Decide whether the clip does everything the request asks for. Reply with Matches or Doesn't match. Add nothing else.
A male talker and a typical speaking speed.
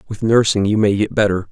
Doesn't match